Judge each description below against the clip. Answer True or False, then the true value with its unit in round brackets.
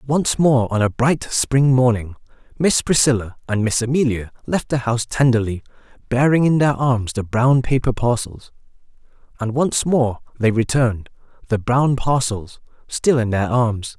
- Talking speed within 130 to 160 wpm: True (150 wpm)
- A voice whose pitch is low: True (125 Hz)